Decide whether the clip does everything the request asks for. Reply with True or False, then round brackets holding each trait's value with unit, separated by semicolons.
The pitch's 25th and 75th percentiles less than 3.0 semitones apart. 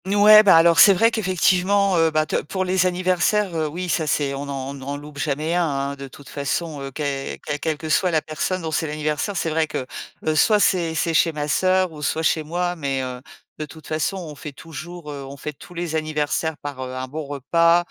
False (3.5 semitones)